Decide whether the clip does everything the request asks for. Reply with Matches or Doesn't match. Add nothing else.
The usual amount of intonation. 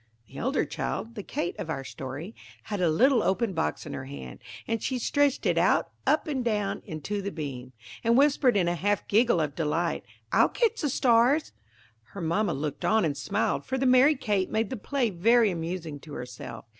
Doesn't match